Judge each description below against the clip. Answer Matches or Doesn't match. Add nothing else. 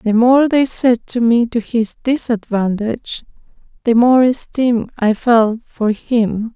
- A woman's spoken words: Matches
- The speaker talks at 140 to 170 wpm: Matches